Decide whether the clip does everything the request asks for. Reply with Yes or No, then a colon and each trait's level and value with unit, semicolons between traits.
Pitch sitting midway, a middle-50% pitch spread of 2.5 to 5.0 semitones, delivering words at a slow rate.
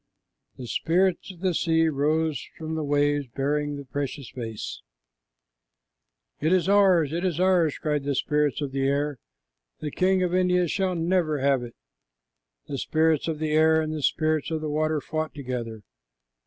No: medium, 155 Hz; average, 2.8 semitones; average, 170 wpm